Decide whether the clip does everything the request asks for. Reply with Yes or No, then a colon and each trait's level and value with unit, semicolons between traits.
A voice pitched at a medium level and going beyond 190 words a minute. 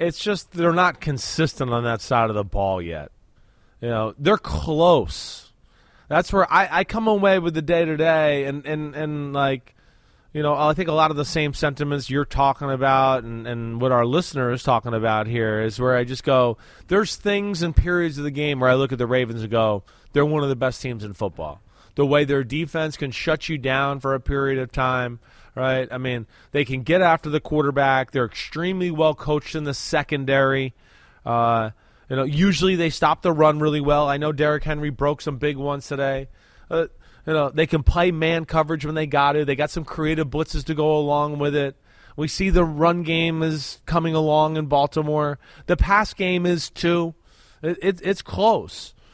Yes: medium, 145 Hz; fast, 205 wpm